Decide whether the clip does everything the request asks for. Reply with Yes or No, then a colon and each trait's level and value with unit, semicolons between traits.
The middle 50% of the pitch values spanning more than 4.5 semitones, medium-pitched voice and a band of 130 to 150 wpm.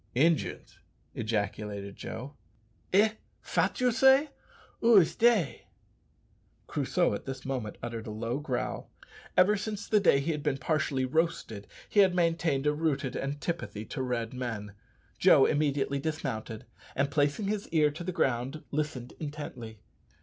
Yes: wide, 5.6 semitones; medium, 145 Hz; average, 140 wpm